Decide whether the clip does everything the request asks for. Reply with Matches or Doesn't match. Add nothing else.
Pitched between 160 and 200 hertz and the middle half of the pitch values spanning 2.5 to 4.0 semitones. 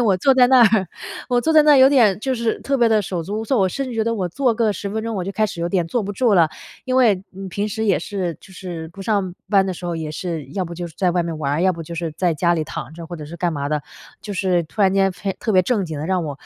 Doesn't match